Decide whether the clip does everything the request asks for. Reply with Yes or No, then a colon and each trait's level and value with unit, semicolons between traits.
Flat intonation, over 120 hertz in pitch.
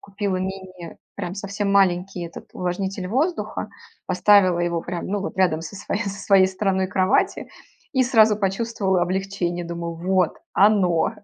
Yes: narrow, 2.1 semitones; high, 190 Hz